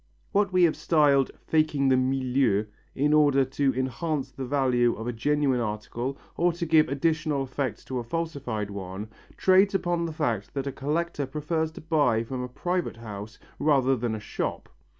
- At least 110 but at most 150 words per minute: No, average, 175 wpm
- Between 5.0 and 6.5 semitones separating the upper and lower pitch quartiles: No, average, 4.3 semitones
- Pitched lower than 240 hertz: Yes, low, 135 Hz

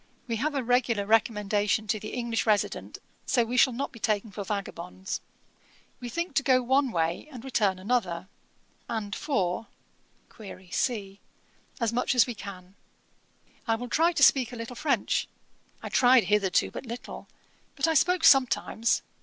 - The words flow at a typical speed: Yes, average, 160 wpm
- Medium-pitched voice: No, high, 230 Hz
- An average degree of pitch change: Yes, average, 3.9 semitones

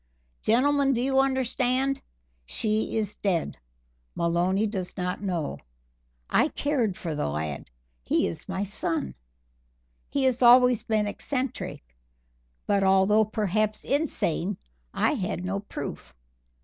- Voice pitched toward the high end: Yes, high, 210 Hz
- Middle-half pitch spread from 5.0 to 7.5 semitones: Yes, wide, 5.5 semitones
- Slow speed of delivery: Yes, slow, 120 wpm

